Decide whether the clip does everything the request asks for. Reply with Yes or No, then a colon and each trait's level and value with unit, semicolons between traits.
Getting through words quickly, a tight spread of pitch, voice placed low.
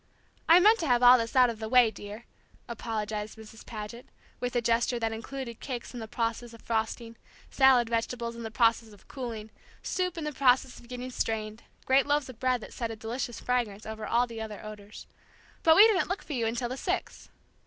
No: fast, 210 wpm; narrow, 2.3 semitones; high, 235 Hz